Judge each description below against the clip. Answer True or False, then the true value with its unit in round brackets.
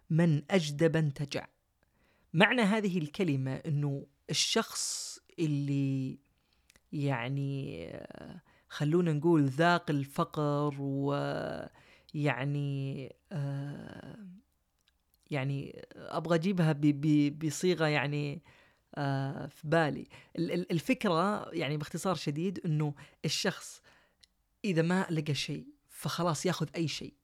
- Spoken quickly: False (90 wpm)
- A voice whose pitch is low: False (150 Hz)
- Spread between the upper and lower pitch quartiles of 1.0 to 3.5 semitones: True (3.1 semitones)